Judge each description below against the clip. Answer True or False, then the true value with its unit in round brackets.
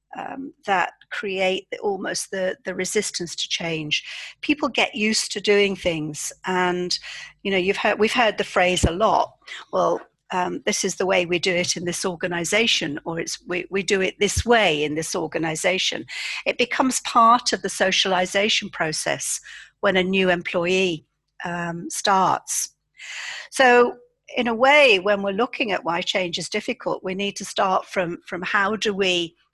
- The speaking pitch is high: True (195 Hz)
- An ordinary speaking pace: True (170 wpm)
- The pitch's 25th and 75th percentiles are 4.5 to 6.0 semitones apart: False (3.4 semitones)